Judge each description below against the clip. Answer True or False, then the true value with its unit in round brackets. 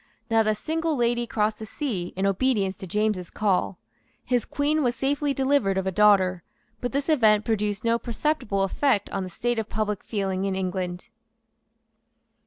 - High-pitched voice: True (215 Hz)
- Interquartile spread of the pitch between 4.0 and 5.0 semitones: True (4.3 semitones)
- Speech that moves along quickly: False (170 wpm)